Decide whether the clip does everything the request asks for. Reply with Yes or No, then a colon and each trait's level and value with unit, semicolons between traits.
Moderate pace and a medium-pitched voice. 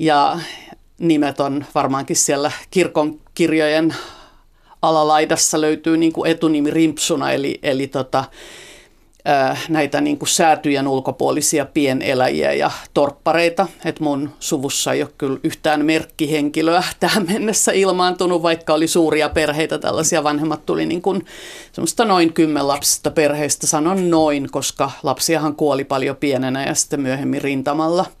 Yes: average, 125 wpm; medium, 155 Hz